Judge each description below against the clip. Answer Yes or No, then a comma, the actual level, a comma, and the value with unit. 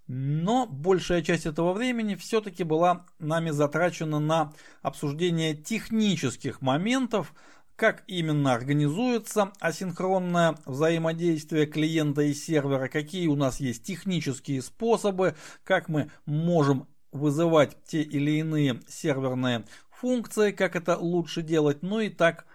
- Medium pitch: Yes, medium, 165 Hz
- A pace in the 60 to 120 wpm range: Yes, average, 115 wpm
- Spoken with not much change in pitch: No, average, 4.1 semitones